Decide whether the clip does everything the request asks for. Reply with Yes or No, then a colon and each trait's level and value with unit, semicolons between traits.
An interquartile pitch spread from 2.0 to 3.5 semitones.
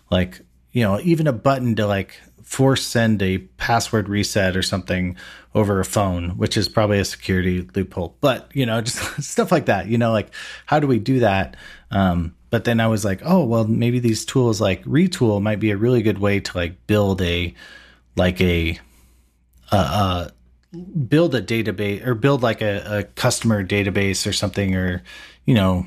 No: average, 4.1 semitones